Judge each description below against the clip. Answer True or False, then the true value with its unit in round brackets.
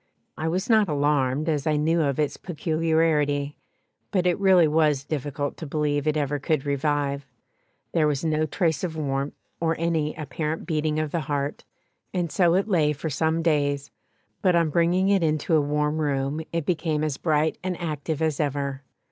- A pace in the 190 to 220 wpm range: False (180 wpm)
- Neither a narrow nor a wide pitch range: False (2.3 semitones)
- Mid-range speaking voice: True (155 Hz)